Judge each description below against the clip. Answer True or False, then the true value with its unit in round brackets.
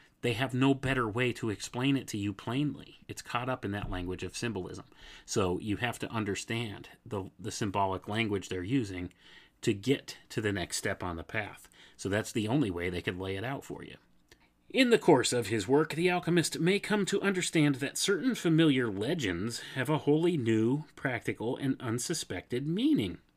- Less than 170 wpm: False (195 wpm)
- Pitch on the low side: True (120 Hz)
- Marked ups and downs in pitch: True (6.0 semitones)